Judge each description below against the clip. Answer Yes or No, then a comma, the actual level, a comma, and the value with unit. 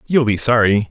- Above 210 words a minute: No, average, 200 wpm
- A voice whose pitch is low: Yes, low, 115 Hz